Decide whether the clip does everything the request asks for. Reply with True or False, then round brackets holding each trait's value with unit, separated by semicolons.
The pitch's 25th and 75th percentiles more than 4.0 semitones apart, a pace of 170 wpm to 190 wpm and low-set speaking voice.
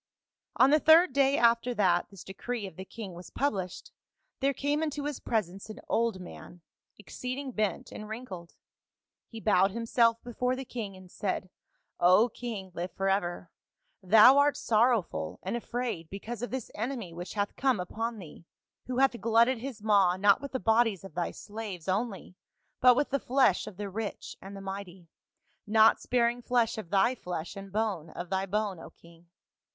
False (4.4 semitones; 180 wpm; 215 Hz)